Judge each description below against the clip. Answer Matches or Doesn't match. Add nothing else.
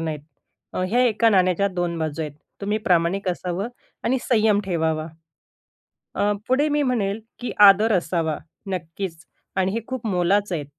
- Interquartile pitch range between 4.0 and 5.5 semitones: Matches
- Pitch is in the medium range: Doesn't match